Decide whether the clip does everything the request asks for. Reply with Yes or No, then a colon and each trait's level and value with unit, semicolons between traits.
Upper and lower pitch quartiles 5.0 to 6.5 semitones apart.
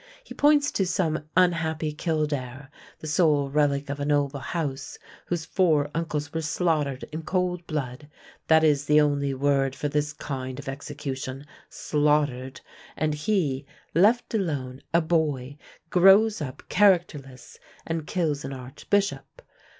No: average, 3.2 semitones